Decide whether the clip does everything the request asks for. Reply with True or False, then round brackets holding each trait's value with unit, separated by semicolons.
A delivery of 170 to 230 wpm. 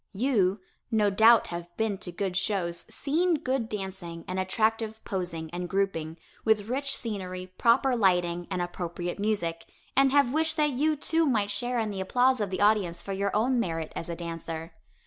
True (180 wpm)